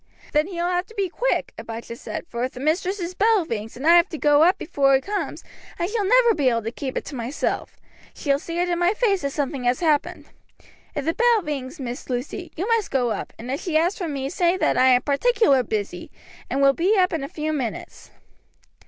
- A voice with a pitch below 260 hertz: No, very high, 310 Hz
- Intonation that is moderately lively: No, wide, 5.7 semitones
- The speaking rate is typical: No, fast, 240 wpm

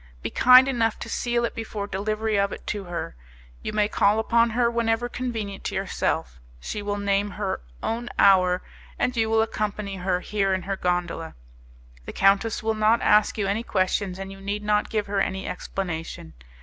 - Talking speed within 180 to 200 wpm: Yes, average, 190 wpm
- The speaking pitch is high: Yes, high, 205 Hz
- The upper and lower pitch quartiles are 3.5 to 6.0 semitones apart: No, narrow, 2.5 semitones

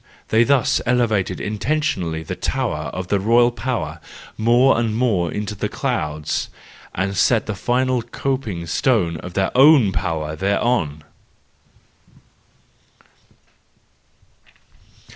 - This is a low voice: Yes, low, 105 Hz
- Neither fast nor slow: No, slow, 105 wpm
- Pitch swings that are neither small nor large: No, wide, 5.8 semitones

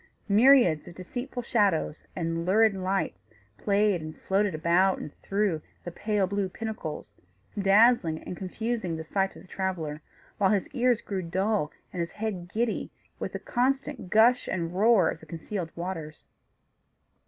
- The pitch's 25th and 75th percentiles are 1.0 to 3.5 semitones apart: No, average, 4.3 semitones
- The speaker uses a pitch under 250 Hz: Yes, high, 190 Hz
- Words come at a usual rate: Yes, average, 155 wpm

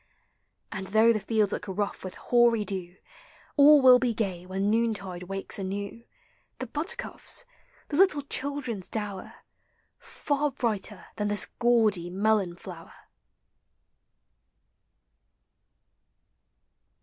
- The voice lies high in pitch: Yes, high, 215 Hz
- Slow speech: Yes, slow, 105 wpm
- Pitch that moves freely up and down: No, average, 4.1 semitones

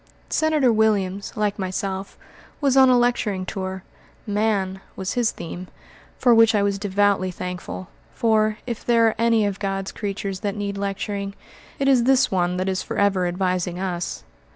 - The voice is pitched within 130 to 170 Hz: No, high, 200 Hz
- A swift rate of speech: No, average, 160 wpm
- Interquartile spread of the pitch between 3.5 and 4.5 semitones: No, average, 2.9 semitones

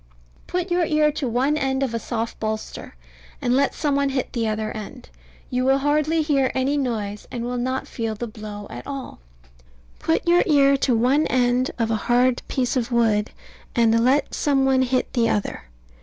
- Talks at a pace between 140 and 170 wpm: No, average, 190 wpm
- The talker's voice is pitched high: Yes, very high, 250 Hz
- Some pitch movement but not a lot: Yes, average, 3.3 semitones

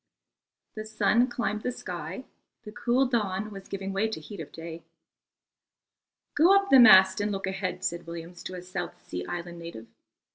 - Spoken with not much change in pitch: No, average, 3.9 semitones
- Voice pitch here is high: Yes, high, 195 Hz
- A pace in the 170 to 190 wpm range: Yes, average, 180 wpm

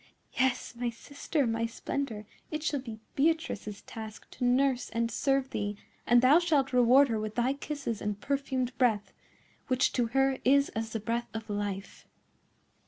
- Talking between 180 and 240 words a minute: No, average, 165 wpm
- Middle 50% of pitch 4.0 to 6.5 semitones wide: No, average, 3.5 semitones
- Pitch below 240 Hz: No, high, 245 Hz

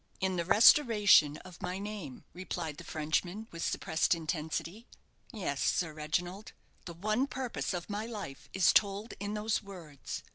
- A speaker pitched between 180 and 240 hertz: Yes, medium, 185 Hz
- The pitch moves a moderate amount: Yes, average, 4.5 semitones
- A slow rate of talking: No, average, 150 wpm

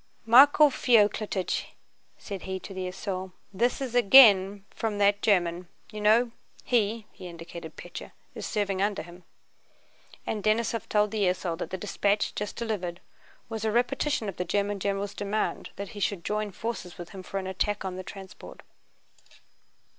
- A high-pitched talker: Yes, high, 205 Hz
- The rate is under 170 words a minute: Yes, average, 155 wpm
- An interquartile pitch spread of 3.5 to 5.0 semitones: No, narrow, 2.6 semitones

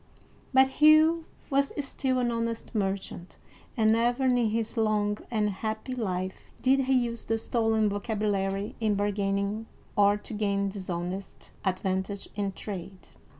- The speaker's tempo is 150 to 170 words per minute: No, slow, 135 wpm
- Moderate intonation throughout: Yes, average, 3.1 semitones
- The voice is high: Yes, high, 215 Hz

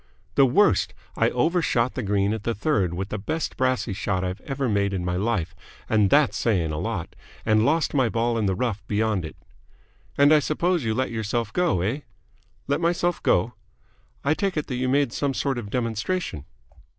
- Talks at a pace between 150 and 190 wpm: No, average, 200 wpm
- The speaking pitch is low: Yes, low, 115 Hz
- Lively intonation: Yes, wide, 5.9 semitones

